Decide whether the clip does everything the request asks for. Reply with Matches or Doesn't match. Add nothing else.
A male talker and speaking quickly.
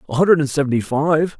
Matches